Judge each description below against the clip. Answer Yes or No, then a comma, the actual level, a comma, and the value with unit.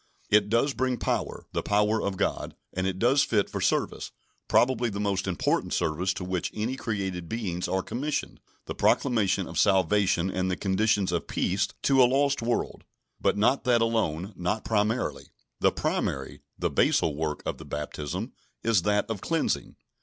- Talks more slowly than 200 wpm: Yes, average, 170 wpm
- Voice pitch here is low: Yes, low, 105 Hz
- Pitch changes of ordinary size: Yes, average, 4.0 semitones